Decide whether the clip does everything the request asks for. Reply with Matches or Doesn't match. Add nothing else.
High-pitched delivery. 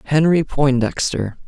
Doesn't match